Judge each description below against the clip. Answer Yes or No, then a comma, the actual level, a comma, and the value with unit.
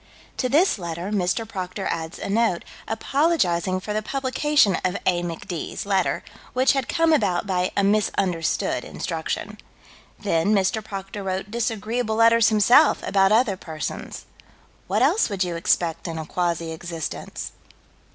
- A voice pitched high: Yes, high, 195 Hz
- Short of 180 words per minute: Yes, average, 150 wpm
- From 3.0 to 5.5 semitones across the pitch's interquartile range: Yes, average, 4.5 semitones